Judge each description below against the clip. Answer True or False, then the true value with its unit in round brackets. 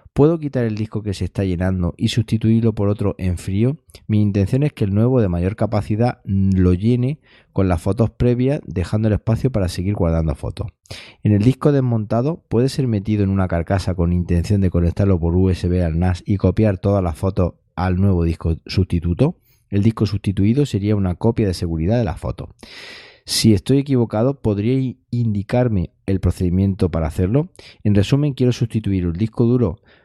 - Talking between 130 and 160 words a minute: False (180 wpm)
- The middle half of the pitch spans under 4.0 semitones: False (4.3 semitones)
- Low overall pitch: True (105 Hz)